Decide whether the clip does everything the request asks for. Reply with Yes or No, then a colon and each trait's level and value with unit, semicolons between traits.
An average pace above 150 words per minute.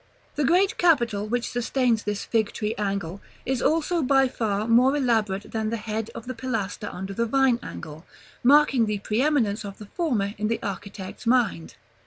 Yes: average, 175 wpm